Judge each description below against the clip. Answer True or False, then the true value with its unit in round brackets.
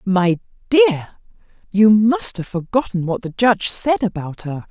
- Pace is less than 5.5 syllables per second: True (4.7 syllables/s)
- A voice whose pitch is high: True (205 Hz)